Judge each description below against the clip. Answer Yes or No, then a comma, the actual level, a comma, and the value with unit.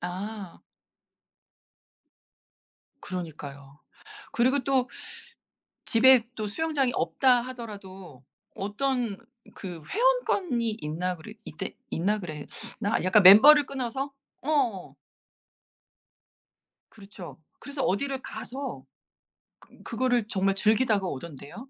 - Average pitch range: No, wide, 6.1 semitones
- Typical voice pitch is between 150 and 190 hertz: No, high, 215 Hz